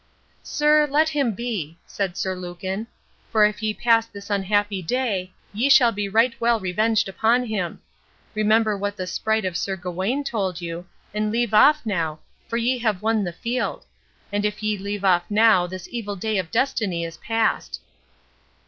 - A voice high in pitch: Yes, high, 210 Hz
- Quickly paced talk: No, average, 175 wpm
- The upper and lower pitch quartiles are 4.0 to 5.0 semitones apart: No, average, 3.5 semitones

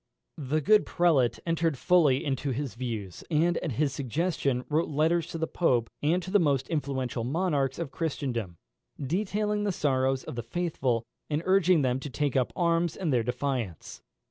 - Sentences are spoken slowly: No, average, 170 wpm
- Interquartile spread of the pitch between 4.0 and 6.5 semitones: Yes, average, 4.6 semitones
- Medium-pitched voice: Yes, medium, 145 Hz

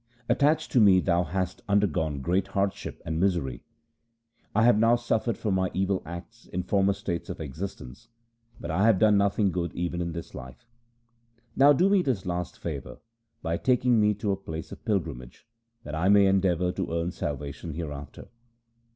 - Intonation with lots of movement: No, average, 4.0 semitones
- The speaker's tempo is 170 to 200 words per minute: Yes, average, 175 wpm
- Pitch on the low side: Yes, very low, 95 Hz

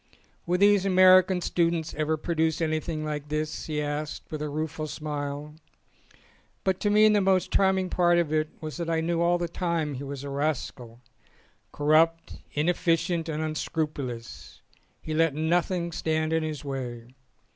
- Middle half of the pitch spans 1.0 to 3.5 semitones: Yes, narrow, 2.4 semitones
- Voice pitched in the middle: Yes, medium, 160 Hz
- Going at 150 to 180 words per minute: Yes, average, 165 wpm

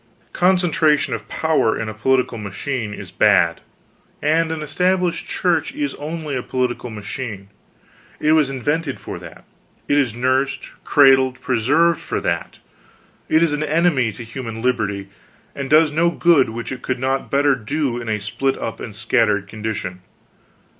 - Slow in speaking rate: No, average, 155 wpm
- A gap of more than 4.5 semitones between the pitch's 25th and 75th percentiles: Yes, wide, 5.5 semitones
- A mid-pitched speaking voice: No, low, 130 Hz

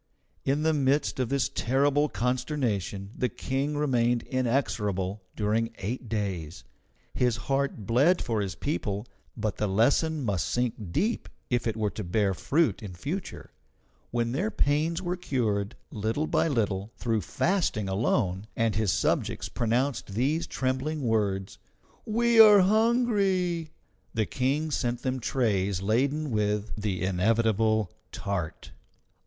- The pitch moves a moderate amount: No, wide, 5.7 semitones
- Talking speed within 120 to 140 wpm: Yes, slow, 135 wpm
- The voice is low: Yes, low, 120 Hz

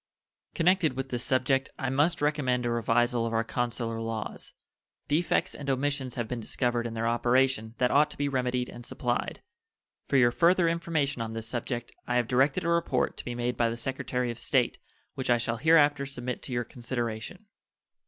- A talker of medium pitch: No, low, 125 Hz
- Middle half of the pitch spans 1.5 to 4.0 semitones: Yes, average, 2.8 semitones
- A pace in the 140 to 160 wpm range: No, average, 190 wpm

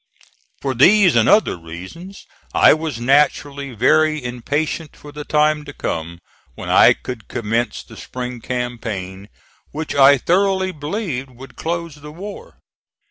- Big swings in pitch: No, average, 4.6 semitones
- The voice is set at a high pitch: No, medium, 140 Hz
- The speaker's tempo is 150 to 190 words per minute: No, slow, 135 wpm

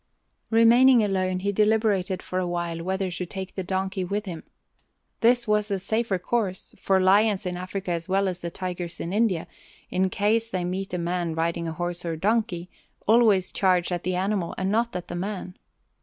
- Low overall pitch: No, high, 190 Hz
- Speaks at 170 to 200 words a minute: Yes, average, 190 wpm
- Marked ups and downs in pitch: No, average, 2.8 semitones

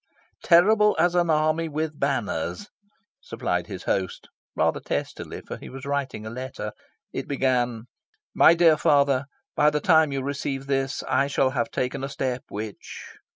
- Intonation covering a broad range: No, average, 3.2 semitones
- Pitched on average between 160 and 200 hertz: No, medium, 140 Hz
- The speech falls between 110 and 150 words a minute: No, average, 160 wpm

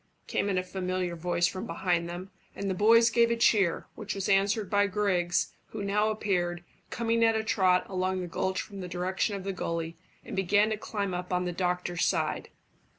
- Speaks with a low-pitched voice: No, high, 190 Hz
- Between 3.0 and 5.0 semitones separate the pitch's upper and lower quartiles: No, narrow, 2.5 semitones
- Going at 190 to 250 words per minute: Yes, fast, 205 wpm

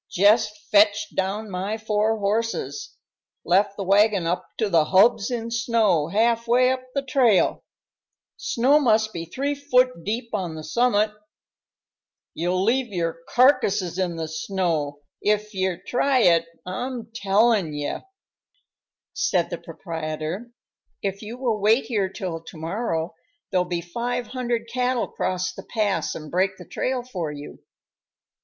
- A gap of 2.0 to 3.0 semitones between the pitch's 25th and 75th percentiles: No, average, 4.8 semitones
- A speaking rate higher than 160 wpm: No, average, 145 wpm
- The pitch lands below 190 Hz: No, high, 210 Hz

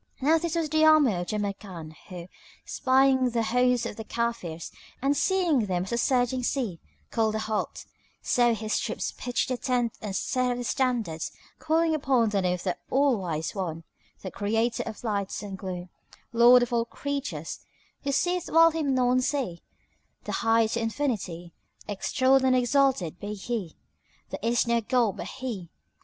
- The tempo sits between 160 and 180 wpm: Yes, average, 175 wpm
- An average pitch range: Yes, average, 4.6 semitones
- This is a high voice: Yes, high, 235 Hz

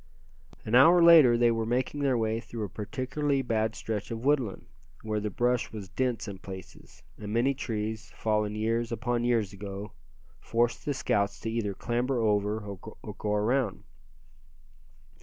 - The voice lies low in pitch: Yes, low, 115 Hz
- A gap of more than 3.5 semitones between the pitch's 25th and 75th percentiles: No, average, 2.8 semitones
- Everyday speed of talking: Yes, average, 160 wpm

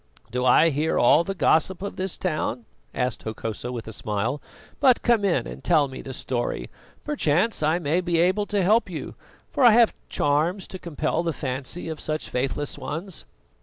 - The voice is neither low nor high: Yes, medium, 160 Hz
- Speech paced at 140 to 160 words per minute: No, average, 185 wpm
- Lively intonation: Yes, wide, 5.9 semitones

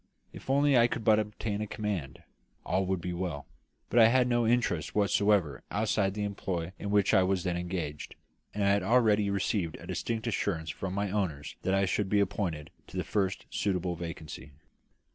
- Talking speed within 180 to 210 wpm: Yes, average, 190 wpm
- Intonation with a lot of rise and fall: No, average, 3.2 semitones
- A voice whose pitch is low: Yes, low, 100 Hz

